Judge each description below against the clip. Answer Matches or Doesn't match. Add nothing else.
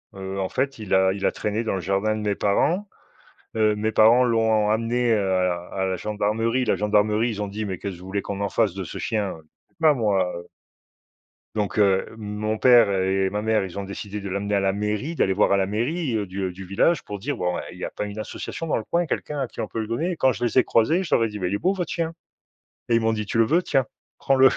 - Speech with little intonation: Doesn't match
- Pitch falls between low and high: Doesn't match